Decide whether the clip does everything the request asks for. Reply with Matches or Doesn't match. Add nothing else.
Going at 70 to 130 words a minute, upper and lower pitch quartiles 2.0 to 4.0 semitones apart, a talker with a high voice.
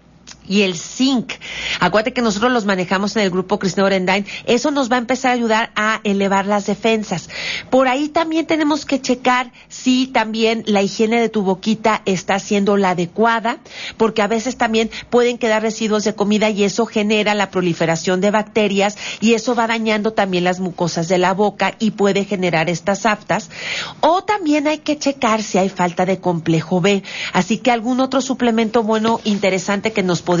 Doesn't match